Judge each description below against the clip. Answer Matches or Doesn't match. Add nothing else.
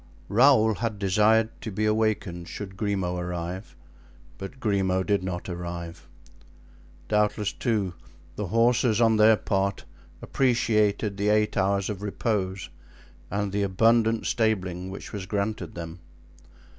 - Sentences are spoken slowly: Matches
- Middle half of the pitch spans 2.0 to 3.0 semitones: Matches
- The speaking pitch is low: Matches